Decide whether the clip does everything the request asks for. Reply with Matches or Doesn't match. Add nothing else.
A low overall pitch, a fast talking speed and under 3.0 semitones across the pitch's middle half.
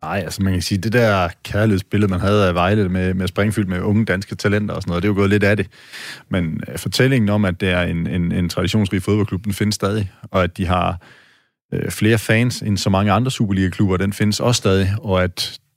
Matches